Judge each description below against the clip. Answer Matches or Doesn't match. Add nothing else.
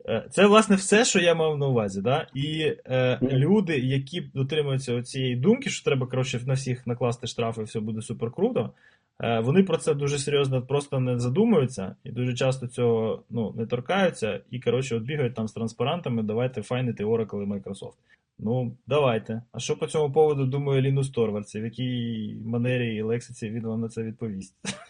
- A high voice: Doesn't match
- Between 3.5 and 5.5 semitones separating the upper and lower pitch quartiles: Matches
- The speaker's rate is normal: Doesn't match